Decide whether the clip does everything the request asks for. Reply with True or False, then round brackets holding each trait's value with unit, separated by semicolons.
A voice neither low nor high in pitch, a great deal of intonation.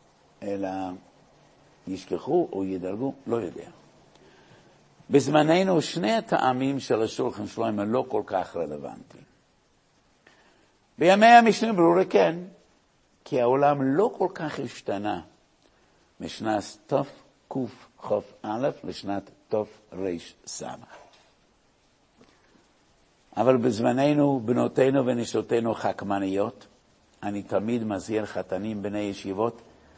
False (115 Hz; 5.7 semitones)